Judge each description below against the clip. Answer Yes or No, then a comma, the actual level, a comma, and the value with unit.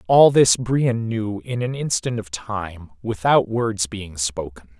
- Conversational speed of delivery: Yes, average, 165 wpm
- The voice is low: Yes, low, 105 Hz